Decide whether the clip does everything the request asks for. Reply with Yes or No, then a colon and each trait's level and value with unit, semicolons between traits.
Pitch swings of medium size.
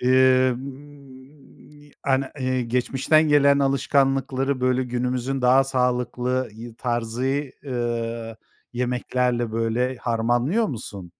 No: narrow, 2.0 semitones